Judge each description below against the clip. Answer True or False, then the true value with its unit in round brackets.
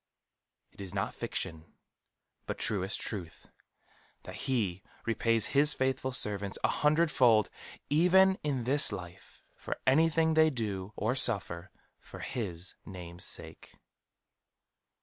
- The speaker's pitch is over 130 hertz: False (115 Hz)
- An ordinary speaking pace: False (120 wpm)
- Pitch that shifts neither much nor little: False (7.3 semitones)